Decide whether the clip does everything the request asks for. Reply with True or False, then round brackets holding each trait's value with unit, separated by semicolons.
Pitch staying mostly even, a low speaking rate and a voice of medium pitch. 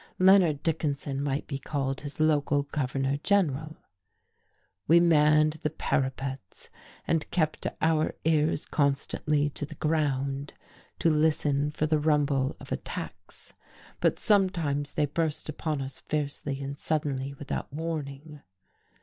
True (2.0 semitones; 125 wpm; 150 Hz)